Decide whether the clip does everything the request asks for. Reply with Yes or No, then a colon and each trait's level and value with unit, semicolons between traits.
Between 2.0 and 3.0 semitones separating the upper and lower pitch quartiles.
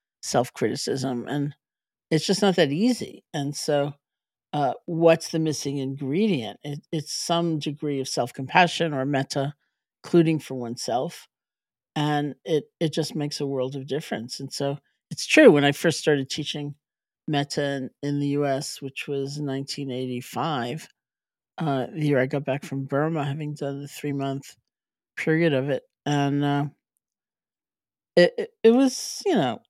Yes: narrow, 2.6 semitones